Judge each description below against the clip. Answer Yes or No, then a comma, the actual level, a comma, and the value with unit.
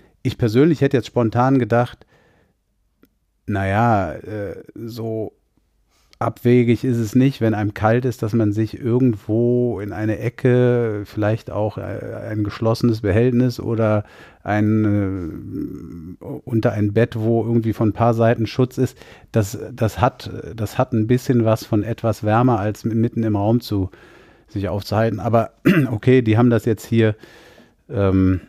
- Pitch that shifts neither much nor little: No, narrow, 2.2 semitones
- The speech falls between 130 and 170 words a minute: Yes, average, 140 wpm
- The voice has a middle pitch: No, low, 115 Hz